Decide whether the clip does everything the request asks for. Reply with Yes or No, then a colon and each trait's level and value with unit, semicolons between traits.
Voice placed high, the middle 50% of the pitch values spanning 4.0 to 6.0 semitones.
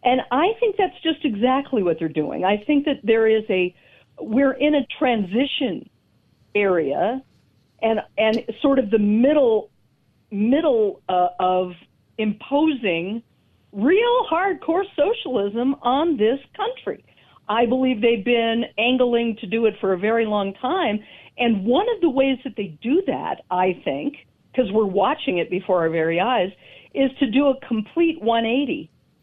Yes: high, 245 Hz; wide, 5.4 semitones